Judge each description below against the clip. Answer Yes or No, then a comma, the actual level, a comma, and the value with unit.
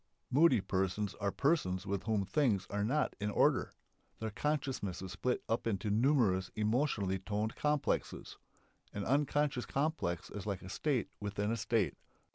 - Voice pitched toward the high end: No, low, 105 Hz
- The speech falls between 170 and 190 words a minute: No, average, 150 wpm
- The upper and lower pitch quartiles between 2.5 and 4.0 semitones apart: No, wide, 5.5 semitones